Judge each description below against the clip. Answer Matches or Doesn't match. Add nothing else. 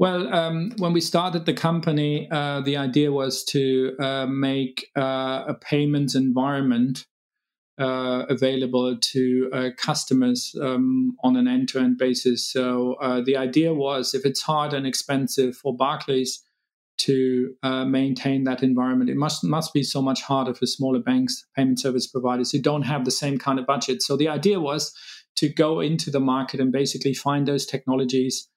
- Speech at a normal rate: Matches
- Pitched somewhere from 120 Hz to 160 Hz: Matches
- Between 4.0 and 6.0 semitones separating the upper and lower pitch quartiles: Doesn't match